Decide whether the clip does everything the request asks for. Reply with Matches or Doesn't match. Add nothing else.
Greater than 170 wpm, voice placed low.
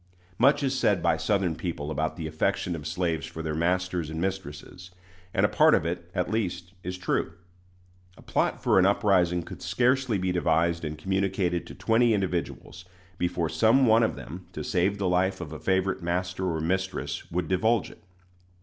Matches